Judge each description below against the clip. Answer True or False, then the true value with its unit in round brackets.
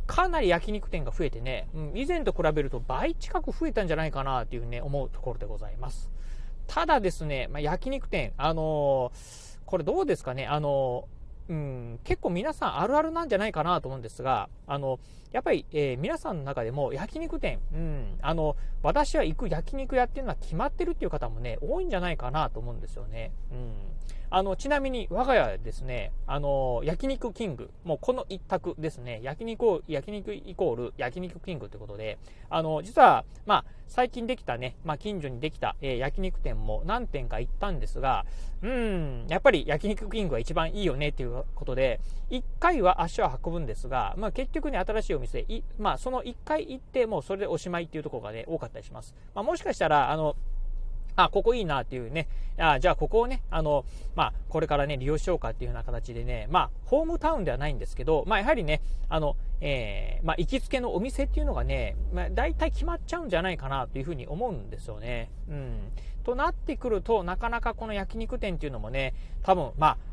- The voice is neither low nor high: True (155 Hz)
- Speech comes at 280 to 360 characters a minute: False (415 characters per minute)